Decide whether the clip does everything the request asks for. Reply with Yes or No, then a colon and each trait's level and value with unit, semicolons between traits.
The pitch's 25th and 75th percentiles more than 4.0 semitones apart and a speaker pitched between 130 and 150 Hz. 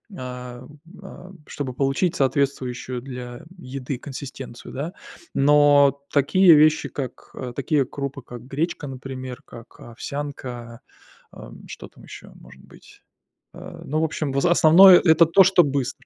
No: average, 3.2 semitones; medium, 140 Hz